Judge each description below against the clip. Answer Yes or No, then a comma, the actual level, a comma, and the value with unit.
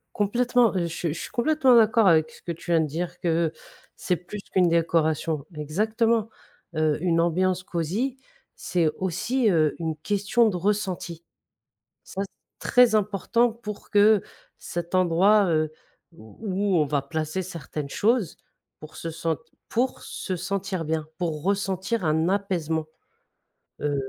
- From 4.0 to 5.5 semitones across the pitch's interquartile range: Yes, average, 4.5 semitones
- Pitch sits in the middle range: Yes, medium, 180 Hz